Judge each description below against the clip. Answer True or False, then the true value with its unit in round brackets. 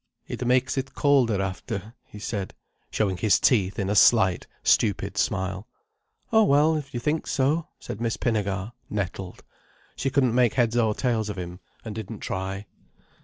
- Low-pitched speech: True (110 Hz)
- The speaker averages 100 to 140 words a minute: False (165 wpm)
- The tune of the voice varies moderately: True (4.7 semitones)